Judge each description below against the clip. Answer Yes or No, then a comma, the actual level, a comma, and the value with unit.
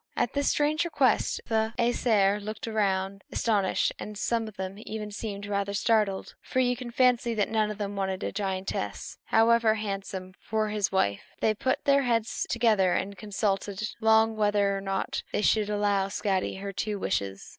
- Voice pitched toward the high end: Yes, high, 210 Hz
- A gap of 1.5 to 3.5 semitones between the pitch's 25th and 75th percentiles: Yes, narrow, 2.4 semitones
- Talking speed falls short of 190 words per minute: Yes, average, 165 wpm